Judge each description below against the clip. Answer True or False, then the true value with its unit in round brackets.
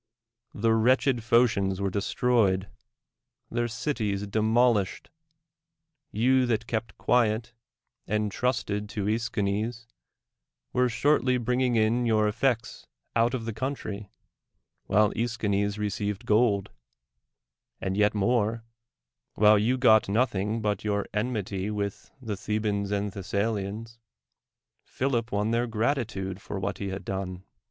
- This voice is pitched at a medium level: False (110 Hz)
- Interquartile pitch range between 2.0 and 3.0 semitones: True (2.7 semitones)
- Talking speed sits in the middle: False (120 wpm)